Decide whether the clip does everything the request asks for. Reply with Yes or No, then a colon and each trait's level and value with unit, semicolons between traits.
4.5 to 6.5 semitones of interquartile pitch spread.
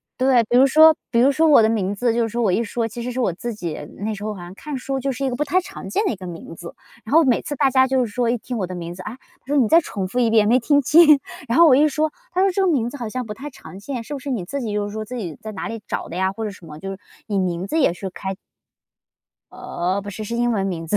Yes: average, 5.2 semitones